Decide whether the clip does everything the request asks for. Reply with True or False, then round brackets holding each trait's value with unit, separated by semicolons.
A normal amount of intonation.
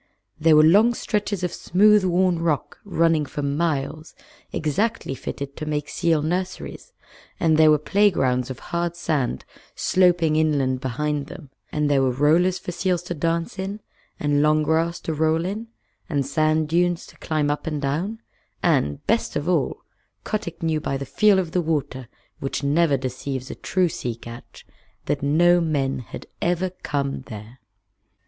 True (3.7 semitones)